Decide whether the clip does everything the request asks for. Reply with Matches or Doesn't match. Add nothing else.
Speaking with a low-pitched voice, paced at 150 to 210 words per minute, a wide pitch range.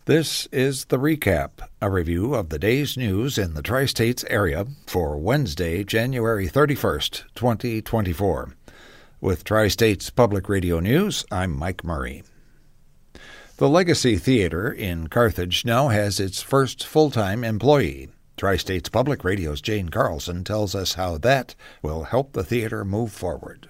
Doesn't match